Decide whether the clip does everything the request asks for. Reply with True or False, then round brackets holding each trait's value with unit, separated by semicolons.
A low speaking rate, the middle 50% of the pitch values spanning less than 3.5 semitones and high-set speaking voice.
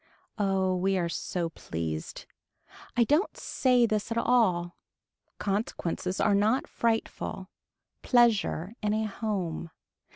False (110 wpm; 4.0 semitones; 200 Hz)